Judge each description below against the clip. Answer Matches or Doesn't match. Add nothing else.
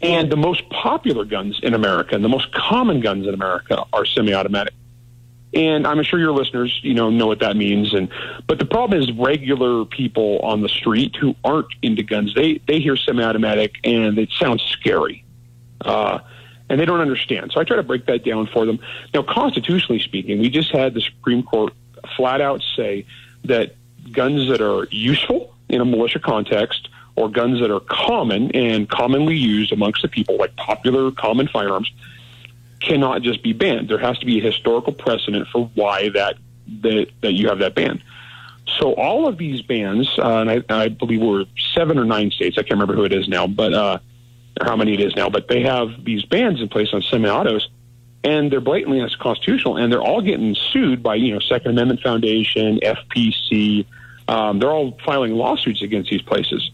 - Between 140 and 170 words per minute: Doesn't match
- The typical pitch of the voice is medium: Doesn't match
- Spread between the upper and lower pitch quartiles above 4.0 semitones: Doesn't match